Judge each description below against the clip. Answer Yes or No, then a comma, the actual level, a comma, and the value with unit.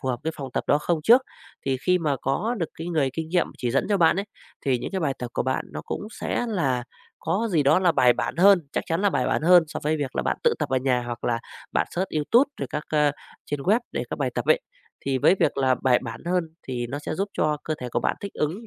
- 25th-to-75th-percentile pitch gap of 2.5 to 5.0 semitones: No, wide, 5.4 semitones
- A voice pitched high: No, medium, 150 Hz